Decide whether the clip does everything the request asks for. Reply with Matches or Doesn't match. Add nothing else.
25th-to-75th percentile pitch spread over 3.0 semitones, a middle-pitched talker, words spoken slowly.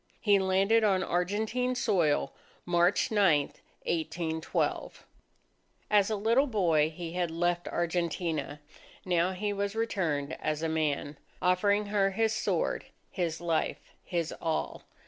Matches